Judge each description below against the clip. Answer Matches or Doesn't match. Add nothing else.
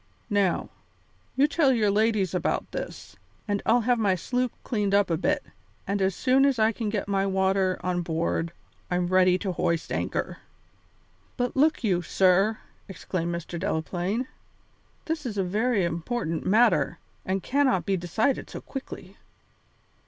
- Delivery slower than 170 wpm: Matches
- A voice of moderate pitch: Doesn't match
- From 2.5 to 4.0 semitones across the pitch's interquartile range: Doesn't match